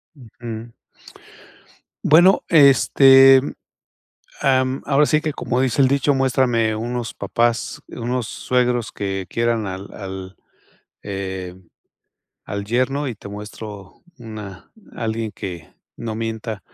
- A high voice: No, low, 115 Hz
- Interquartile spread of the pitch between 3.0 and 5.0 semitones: Yes, average, 4.1 semitones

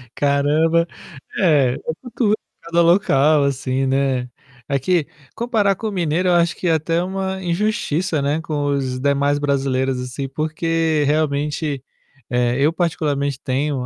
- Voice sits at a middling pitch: Yes, medium, 150 Hz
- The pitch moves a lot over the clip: No, average, 3.5 semitones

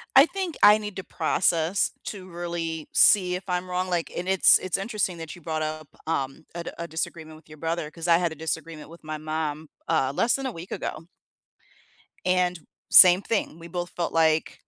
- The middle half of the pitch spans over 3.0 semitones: No, narrow, 2.5 semitones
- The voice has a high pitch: No, medium, 170 Hz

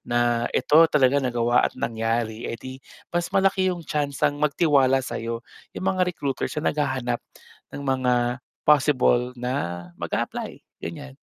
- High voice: No, low, 130 Hz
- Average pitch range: Yes, average, 3.7 semitones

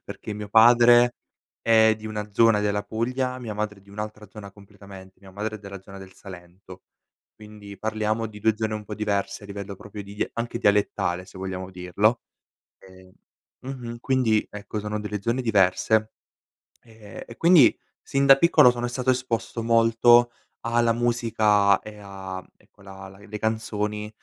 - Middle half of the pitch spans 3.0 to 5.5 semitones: No, narrow, 2.5 semitones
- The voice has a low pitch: Yes, low, 105 Hz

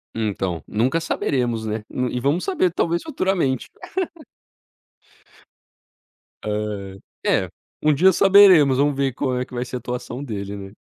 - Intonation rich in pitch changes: Yes, wide, 7.0 semitones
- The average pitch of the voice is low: Yes, low, 130 Hz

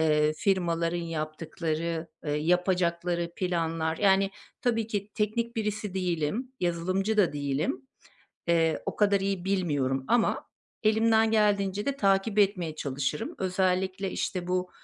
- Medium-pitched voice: Yes, medium, 180 Hz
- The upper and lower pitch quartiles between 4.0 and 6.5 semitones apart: No, average, 3.6 semitones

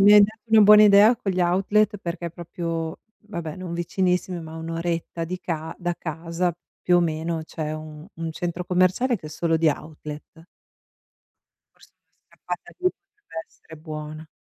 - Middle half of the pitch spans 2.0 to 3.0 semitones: Yes, average, 2.7 semitones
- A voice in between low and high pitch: Yes, medium, 170 Hz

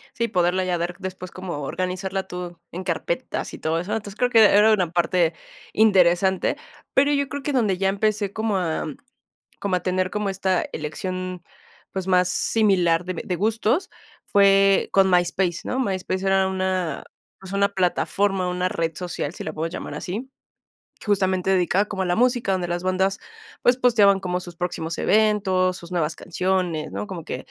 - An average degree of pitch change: No, narrow, 2.1 semitones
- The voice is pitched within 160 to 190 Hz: Yes, medium, 185 Hz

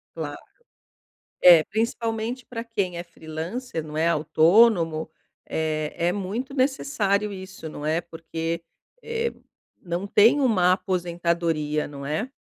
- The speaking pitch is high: No, medium, 175 Hz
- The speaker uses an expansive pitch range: Yes, wide, 5.7 semitones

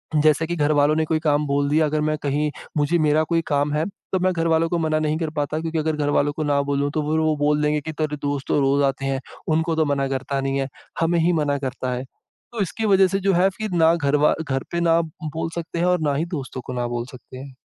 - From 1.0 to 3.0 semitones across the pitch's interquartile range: Yes, narrow, 2.5 semitones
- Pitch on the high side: No, medium, 150 Hz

